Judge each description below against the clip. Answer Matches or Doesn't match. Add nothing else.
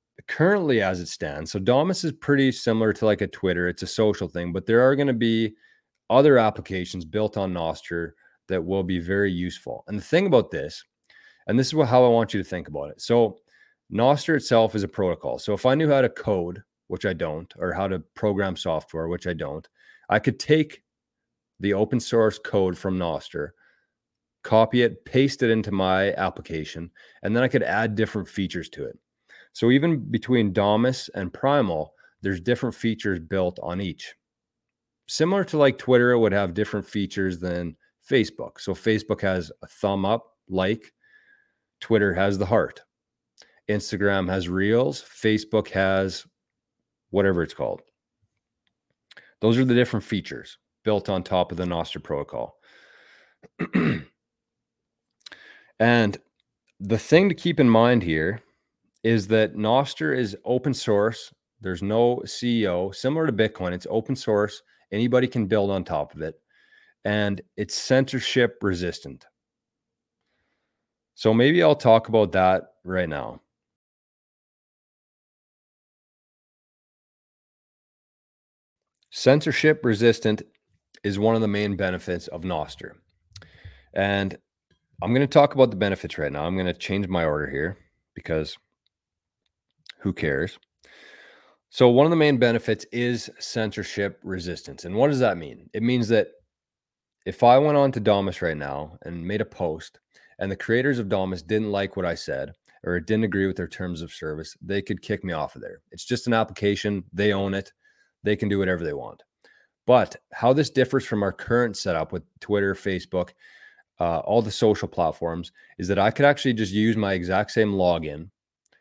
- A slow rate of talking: Doesn't match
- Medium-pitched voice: Doesn't match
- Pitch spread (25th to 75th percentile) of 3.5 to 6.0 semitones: Matches